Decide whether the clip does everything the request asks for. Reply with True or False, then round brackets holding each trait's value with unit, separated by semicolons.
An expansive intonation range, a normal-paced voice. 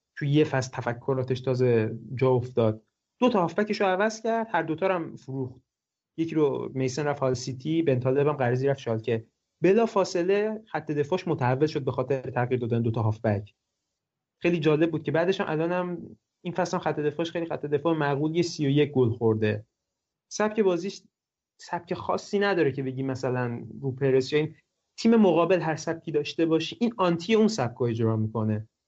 False (5.7 semitones; 185 wpm)